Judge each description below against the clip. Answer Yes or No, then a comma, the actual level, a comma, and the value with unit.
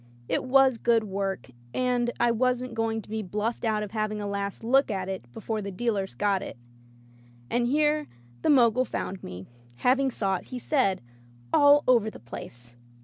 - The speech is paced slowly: No, average, 180 wpm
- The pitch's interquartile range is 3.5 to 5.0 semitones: Yes, average, 4.2 semitones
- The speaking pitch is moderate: No, high, 225 Hz